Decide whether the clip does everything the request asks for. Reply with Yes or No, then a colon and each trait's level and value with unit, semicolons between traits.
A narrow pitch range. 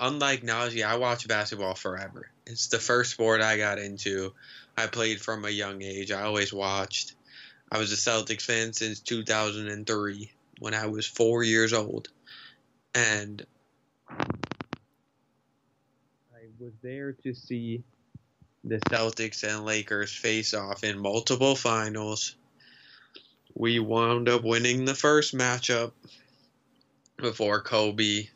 Yes: narrow, 2.3 semitones